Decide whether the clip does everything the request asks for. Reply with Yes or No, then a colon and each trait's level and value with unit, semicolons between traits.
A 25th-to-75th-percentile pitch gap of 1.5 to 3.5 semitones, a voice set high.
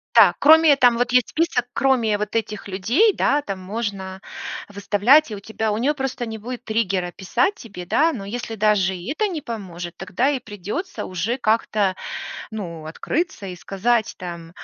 No: average, 4.7 semitones; high, 220 Hz